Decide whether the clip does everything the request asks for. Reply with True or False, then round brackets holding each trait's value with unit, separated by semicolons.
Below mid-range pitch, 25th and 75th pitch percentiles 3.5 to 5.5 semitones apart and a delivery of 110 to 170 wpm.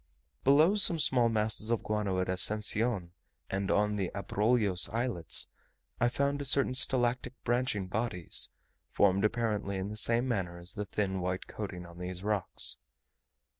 True (105 Hz; 4.2 semitones; 145 wpm)